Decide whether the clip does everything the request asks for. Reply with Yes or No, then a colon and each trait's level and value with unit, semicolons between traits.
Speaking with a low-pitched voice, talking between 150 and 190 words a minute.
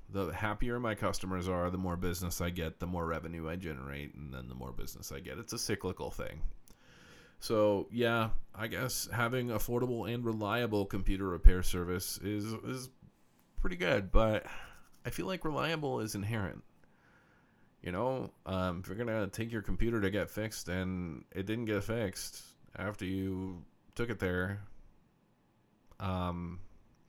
Yes: low, 100 Hz; average, 155 wpm